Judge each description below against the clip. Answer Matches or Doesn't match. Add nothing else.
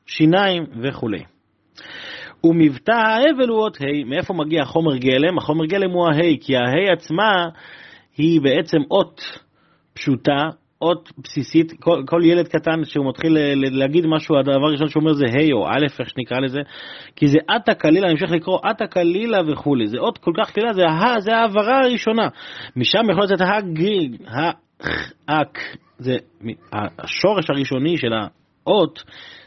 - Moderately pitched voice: Matches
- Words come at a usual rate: Doesn't match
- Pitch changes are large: Doesn't match